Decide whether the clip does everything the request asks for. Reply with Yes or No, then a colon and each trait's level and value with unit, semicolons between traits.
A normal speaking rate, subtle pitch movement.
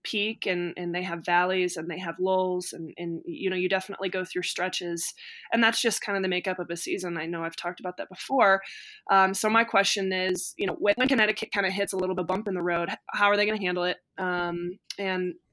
No: fast, 245 wpm; narrow, 2.1 semitones